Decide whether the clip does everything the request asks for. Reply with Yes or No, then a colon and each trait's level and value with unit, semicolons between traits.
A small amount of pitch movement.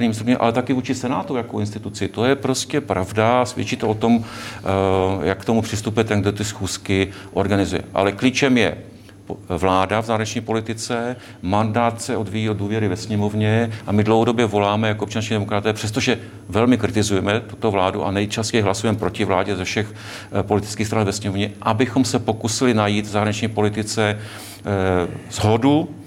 Yes: narrow, 2.3 semitones